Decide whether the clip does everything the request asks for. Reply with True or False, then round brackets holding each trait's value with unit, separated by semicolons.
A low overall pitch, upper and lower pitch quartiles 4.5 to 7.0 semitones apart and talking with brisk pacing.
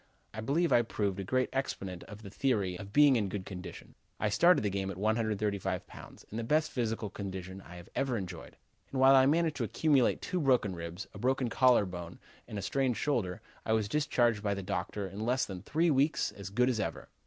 True (110 Hz; 5.3 semitones; 220 wpm)